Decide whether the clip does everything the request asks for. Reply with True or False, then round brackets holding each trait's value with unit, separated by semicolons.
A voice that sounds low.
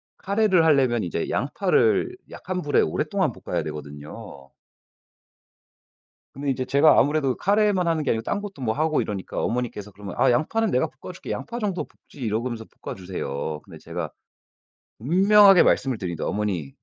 True (130 Hz)